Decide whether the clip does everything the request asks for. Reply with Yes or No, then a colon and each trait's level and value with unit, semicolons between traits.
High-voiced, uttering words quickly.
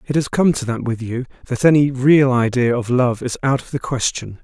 No: low, 125 Hz; fast, 245 wpm